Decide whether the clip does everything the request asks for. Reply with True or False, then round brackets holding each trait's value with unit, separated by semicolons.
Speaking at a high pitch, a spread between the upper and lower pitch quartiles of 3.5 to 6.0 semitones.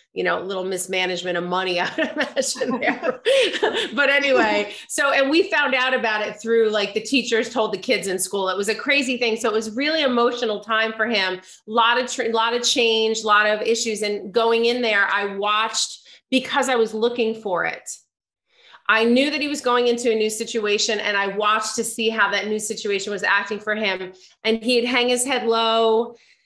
False (225 Hz; 3.0 semitones)